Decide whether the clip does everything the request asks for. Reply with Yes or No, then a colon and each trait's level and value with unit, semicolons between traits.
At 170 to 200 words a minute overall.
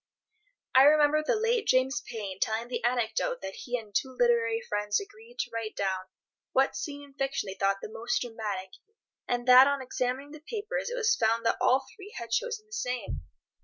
Yes: average, 195 wpm